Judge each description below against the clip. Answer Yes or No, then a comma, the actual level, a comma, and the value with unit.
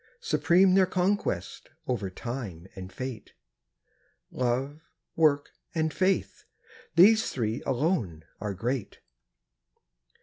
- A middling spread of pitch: No, wide, 8.7 semitones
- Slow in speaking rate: Yes, slow, 90 wpm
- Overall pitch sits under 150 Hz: Yes, low, 135 Hz